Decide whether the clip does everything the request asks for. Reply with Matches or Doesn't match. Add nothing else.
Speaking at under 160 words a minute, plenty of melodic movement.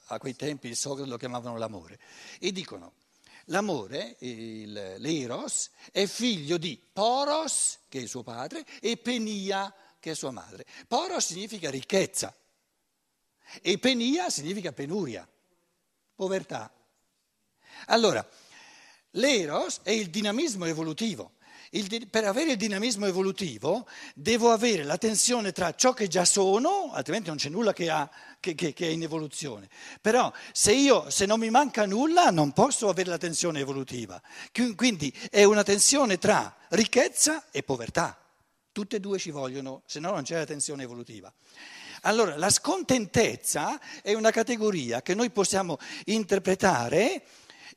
Matches